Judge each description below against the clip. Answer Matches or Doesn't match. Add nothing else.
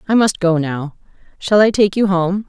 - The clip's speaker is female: Matches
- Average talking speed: Doesn't match